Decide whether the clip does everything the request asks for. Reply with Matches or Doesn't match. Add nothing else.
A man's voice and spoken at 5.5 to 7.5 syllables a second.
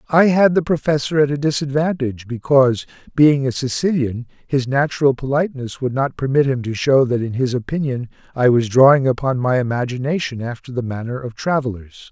Matches